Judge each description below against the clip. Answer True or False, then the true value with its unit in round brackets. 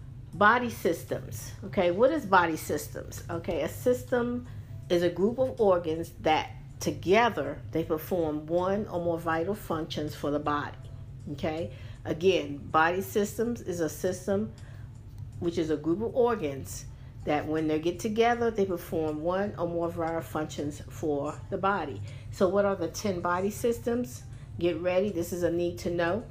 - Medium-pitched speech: True (165 Hz)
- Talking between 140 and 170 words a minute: True (160 wpm)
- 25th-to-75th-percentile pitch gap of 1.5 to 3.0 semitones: False (5.0 semitones)